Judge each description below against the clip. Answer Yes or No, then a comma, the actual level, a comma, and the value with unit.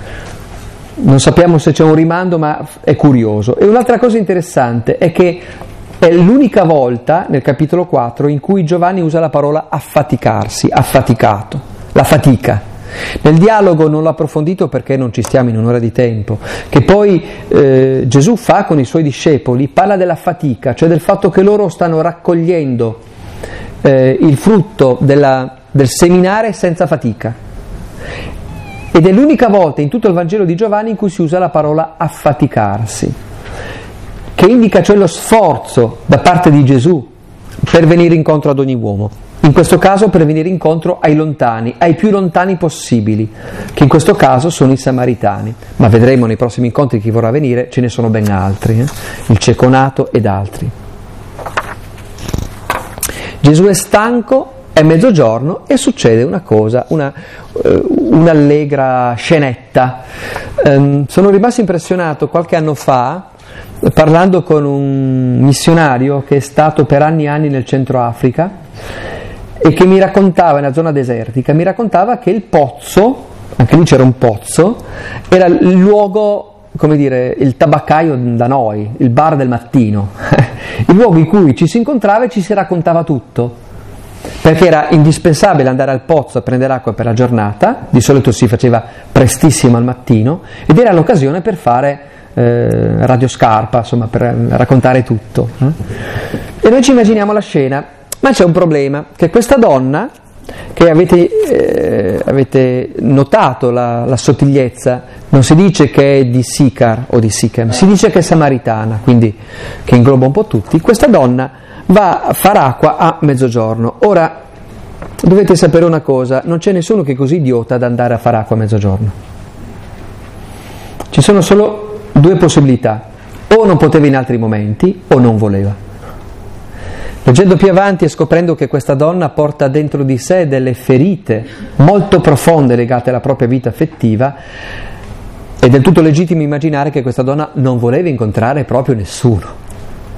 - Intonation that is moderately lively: No, wide, 6.1 semitones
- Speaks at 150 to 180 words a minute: Yes, average, 155 wpm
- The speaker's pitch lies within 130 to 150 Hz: Yes, medium, 140 Hz